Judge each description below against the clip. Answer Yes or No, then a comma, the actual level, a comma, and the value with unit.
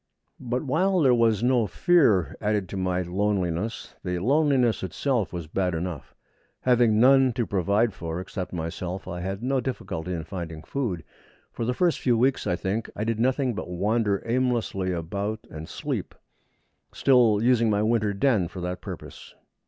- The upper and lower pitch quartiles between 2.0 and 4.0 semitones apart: No, wide, 5.4 semitones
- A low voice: Yes, low, 105 Hz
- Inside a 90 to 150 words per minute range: No, average, 165 wpm